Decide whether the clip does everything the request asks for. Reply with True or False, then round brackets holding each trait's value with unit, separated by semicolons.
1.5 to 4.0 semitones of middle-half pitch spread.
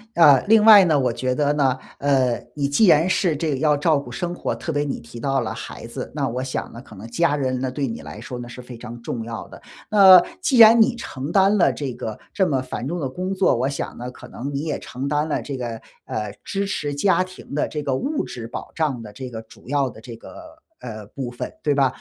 False (5.2 semitones)